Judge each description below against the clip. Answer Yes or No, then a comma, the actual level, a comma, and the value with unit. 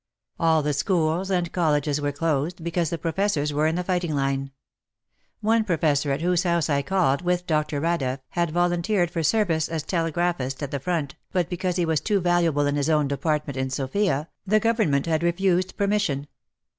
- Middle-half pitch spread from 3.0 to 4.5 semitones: Yes, average, 3.5 semitones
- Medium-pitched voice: Yes, medium, 165 Hz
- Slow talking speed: No, average, 180 wpm